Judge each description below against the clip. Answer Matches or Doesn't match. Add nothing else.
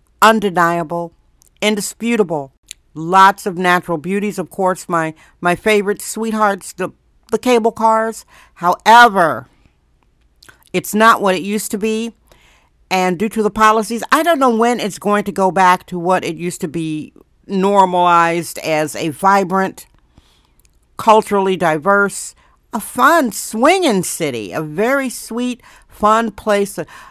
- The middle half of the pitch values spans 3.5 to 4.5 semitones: Matches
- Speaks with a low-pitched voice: Doesn't match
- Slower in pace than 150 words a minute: Matches